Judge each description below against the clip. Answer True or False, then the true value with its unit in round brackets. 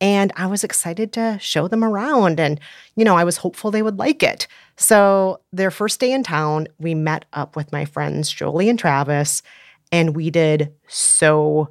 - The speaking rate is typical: True (190 wpm)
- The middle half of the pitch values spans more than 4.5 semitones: True (5.6 semitones)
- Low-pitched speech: False (170 Hz)